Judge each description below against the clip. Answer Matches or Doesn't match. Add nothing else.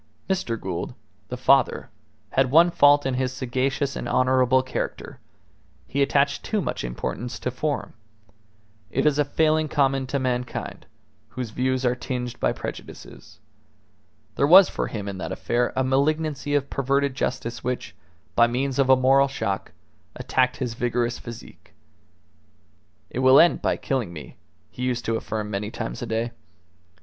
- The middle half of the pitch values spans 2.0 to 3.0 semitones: Matches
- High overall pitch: Doesn't match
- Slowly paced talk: Doesn't match